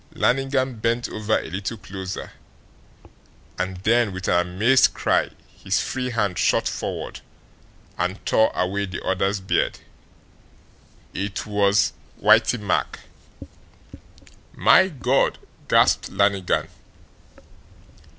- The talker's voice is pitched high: No, low, 100 Hz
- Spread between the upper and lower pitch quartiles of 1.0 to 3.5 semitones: No, average, 4.0 semitones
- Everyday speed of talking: No, slow, 100 wpm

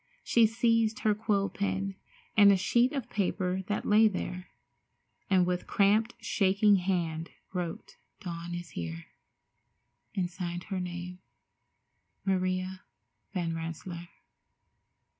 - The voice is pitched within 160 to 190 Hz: Yes, medium, 185 Hz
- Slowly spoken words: Yes, slow, 115 wpm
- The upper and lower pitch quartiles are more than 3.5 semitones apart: No, average, 2.8 semitones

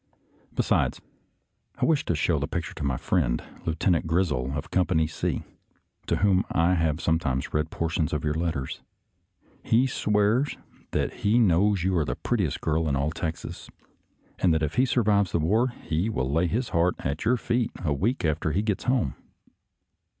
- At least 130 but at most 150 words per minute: No, average, 180 wpm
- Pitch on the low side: Yes, very low, 85 Hz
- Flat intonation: No, average, 5.1 semitones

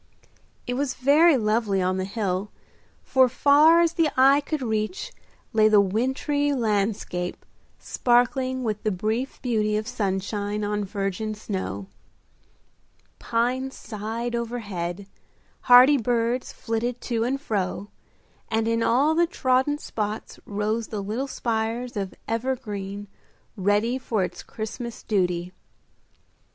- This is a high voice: Yes, high, 225 Hz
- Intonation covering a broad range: No, average, 3.8 semitones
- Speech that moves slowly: Yes, slow, 120 wpm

